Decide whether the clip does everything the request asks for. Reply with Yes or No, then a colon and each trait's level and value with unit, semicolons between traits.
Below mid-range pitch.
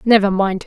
No: high, 200 Hz